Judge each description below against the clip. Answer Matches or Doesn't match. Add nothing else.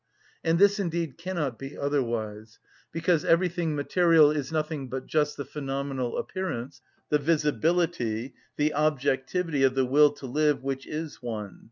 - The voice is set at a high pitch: Doesn't match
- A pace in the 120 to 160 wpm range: Matches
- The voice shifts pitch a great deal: Doesn't match